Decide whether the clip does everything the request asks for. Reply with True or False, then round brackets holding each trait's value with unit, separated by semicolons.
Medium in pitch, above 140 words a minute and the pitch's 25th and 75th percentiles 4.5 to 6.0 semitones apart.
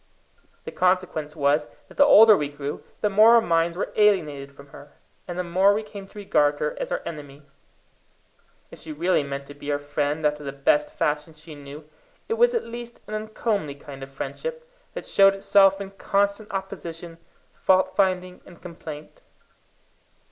True (175 Hz; 175 wpm; 5.5 semitones)